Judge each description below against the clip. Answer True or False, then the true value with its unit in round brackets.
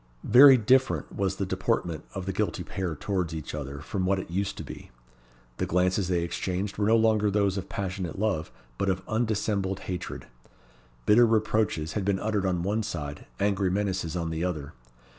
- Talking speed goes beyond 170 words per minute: True (180 wpm)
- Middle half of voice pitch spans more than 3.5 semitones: False (2.9 semitones)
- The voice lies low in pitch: True (95 Hz)